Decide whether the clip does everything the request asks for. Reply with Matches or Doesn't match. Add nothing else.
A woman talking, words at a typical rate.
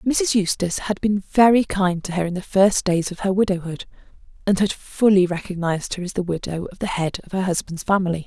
Doesn't match